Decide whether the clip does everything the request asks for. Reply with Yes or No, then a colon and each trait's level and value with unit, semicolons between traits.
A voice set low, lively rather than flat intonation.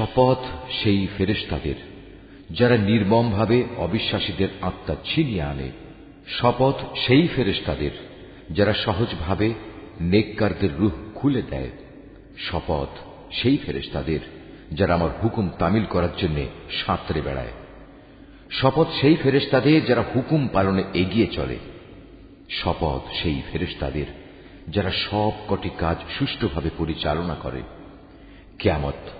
Yes: low, 100 Hz; wide, 6.0 semitones